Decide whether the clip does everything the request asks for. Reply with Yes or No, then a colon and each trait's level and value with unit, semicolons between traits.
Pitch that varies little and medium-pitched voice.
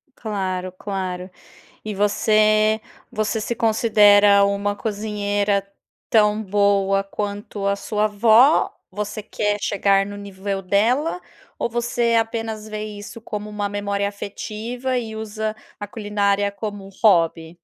No: narrow, 1.4 semitones; high, 205 Hz